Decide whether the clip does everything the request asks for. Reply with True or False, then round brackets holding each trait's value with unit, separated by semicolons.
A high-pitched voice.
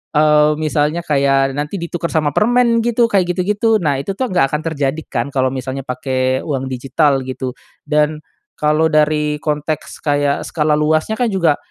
False (150 Hz)